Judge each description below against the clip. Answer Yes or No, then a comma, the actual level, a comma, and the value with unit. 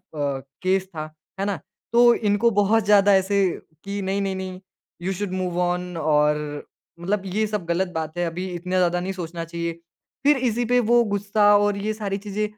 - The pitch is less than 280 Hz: Yes, high, 190 Hz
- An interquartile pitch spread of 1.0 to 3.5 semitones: Yes, average, 2.8 semitones